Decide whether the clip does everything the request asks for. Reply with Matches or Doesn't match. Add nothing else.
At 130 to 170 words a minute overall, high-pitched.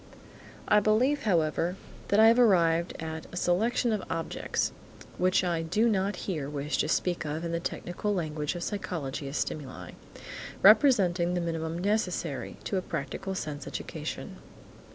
Doesn't match